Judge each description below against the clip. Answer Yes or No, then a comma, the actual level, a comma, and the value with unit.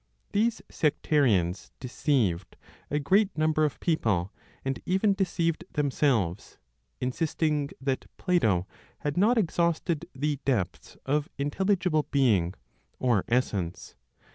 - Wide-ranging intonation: Yes, wide, 6.3 semitones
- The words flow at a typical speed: No, slow, 105 wpm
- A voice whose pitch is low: No, medium, 145 Hz